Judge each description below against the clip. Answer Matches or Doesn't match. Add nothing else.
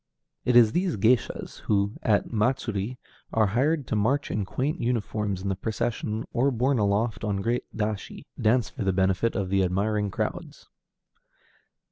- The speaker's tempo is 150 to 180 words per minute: Matches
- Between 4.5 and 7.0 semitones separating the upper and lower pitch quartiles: Doesn't match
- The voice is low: Matches